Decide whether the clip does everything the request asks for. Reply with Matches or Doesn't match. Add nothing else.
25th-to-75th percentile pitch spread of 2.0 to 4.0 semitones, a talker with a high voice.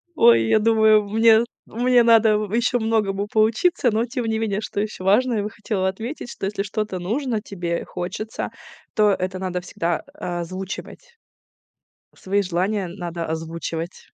Matches